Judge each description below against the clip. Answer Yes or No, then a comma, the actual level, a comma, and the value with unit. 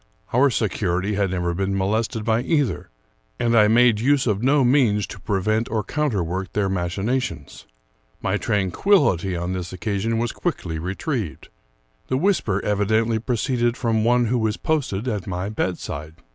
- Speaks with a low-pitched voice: Yes, low, 110 Hz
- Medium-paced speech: Yes, average, 160 wpm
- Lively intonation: No, average, 4.2 semitones